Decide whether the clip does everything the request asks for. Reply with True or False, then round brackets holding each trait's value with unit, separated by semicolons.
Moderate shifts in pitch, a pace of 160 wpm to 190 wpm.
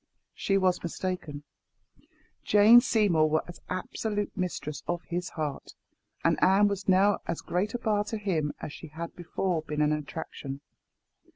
False (4.5 semitones; 150 wpm)